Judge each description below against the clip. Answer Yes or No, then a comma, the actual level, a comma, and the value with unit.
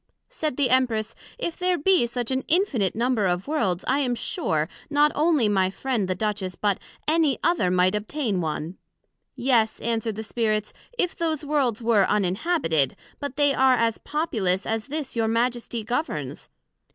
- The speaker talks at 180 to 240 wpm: No, average, 165 wpm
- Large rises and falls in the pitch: Yes, wide, 5.8 semitones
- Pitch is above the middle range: Yes, high, 235 Hz